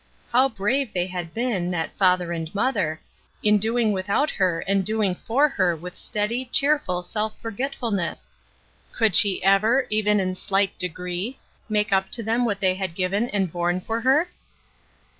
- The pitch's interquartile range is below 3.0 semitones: No, average, 4.0 semitones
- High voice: Yes, high, 200 Hz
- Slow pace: No, average, 170 wpm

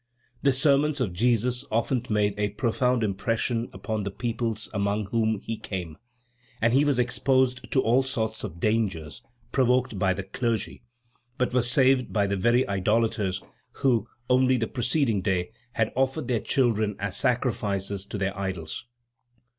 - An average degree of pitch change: Yes, average, 3.9 semitones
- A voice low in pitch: Yes, low, 115 Hz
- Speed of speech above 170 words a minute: No, average, 155 wpm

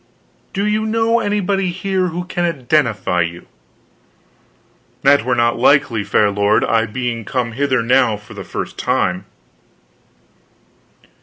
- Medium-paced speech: No, slow, 130 wpm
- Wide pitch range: Yes, wide, 8.3 semitones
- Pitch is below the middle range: Yes, low, 130 Hz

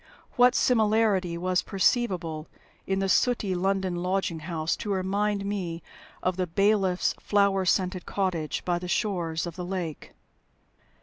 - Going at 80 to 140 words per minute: Yes, slow, 135 wpm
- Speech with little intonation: Yes, narrow, 2.3 semitones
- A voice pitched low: No, medium, 185 Hz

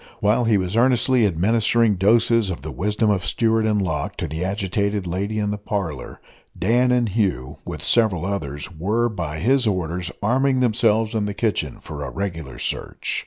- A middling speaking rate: Yes, average, 175 wpm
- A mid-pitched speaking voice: No, low, 105 Hz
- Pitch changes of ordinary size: Yes, average, 3.8 semitones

